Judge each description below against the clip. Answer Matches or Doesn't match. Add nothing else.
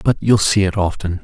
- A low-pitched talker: Matches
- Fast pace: Matches